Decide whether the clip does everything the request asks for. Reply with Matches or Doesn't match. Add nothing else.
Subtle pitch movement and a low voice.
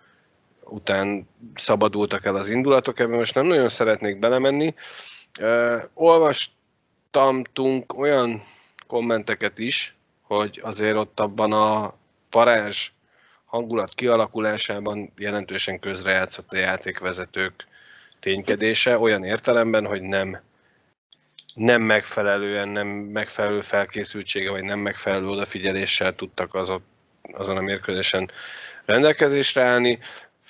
Doesn't match